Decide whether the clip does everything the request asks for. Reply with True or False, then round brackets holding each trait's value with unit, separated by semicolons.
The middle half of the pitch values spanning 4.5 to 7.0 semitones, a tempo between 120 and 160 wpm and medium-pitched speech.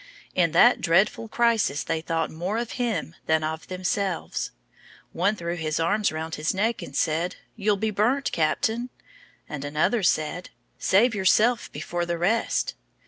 True (5.2 semitones; 150 wpm; 180 Hz)